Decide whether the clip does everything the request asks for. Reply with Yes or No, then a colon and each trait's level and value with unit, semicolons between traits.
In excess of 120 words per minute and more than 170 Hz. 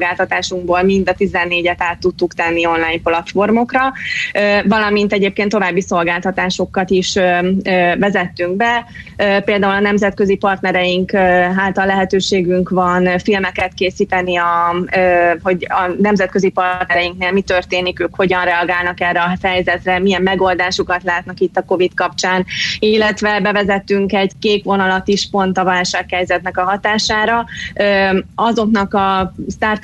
No: average, 115 wpm; high, 190 Hz